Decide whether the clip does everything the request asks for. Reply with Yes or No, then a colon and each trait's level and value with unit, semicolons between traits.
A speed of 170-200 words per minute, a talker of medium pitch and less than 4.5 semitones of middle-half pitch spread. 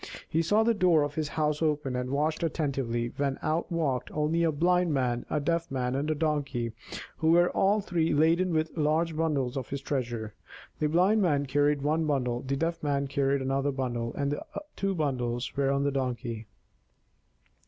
Yes: average, 185 wpm; medium, 145 Hz; average, 3.4 semitones